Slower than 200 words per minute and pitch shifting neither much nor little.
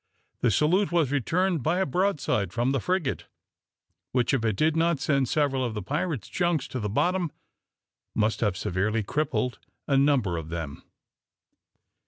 No: average, 160 wpm; wide, 6.8 semitones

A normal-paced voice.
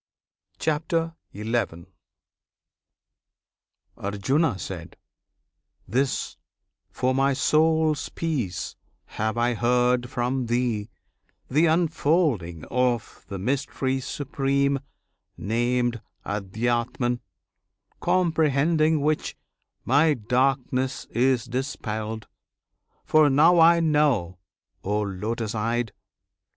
No: slow, 75 wpm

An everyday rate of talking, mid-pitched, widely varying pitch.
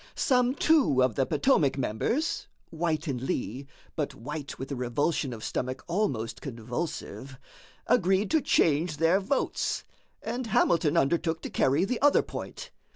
Yes: average, 145 wpm; medium, 155 Hz; wide, 6.7 semitones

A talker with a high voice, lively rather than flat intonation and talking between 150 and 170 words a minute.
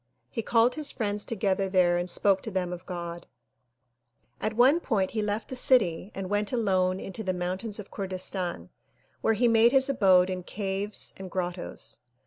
No: high, 195 Hz; average, 3.3 semitones; average, 165 wpm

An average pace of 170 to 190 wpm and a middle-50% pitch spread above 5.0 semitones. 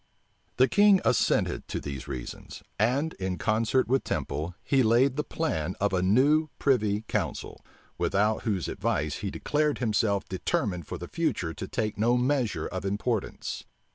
No: average, 155 wpm; wide, 5.5 semitones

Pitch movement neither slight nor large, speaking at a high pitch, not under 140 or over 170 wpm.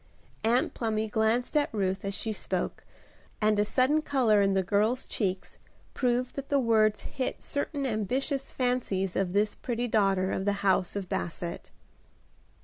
Yes: average, 4.1 semitones; high, 215 Hz; average, 155 wpm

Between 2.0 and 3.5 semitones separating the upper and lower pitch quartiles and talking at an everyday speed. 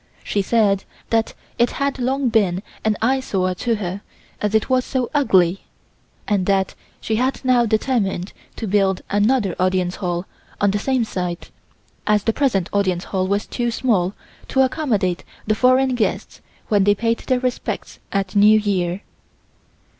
No: average, 4.3 semitones; average, 155 wpm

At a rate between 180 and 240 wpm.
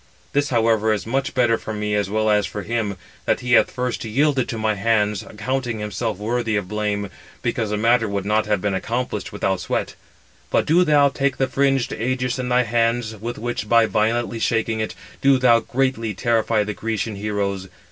Yes: average, 195 wpm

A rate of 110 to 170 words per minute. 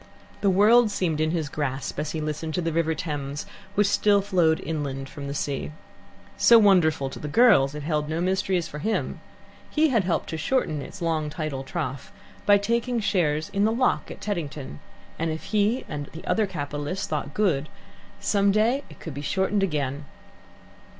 No: average, 180 wpm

